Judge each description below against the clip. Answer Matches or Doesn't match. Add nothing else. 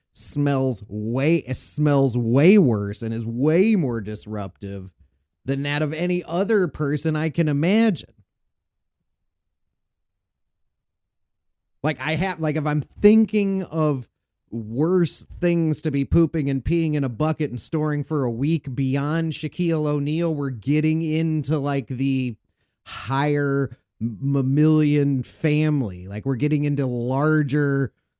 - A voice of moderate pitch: Matches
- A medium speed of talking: Doesn't match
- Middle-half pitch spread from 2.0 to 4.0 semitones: Doesn't match